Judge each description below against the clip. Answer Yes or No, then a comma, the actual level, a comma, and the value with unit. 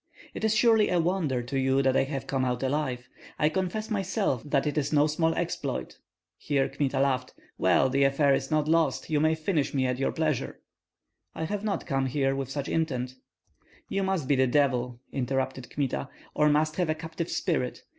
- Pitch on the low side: No, medium, 145 Hz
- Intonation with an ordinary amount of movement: Yes, average, 3.4 semitones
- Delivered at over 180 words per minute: Yes, average, 195 wpm